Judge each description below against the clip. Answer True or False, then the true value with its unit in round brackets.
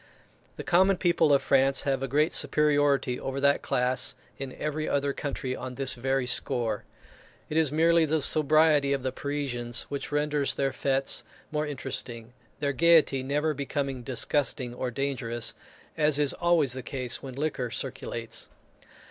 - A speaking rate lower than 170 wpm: True (155 wpm)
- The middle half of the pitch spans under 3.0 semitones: True (2.5 semitones)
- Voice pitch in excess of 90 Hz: True (140 Hz)